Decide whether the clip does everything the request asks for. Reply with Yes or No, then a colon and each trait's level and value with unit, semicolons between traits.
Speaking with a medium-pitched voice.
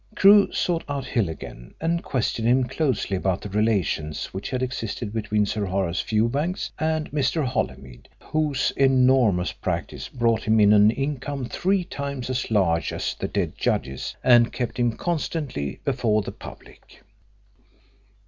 No: low, 120 Hz